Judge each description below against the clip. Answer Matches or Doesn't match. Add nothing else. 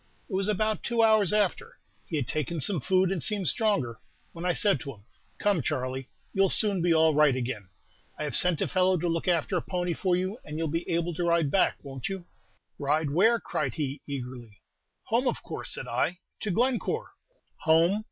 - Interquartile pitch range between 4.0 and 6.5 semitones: Matches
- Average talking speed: Doesn't match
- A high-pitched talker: Doesn't match